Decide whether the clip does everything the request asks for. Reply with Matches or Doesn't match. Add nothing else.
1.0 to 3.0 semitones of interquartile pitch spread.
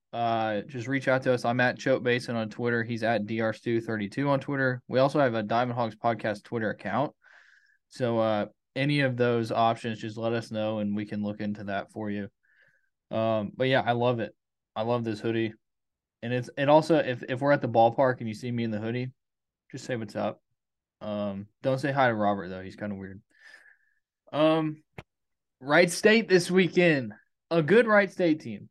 Doesn't match